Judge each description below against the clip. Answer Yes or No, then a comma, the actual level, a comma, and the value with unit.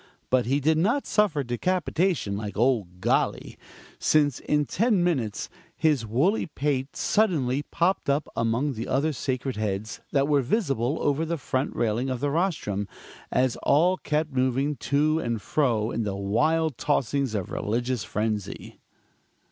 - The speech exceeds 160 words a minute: No, average, 150 wpm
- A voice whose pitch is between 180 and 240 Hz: No, low, 135 Hz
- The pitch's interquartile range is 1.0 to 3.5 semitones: No, average, 5.1 semitones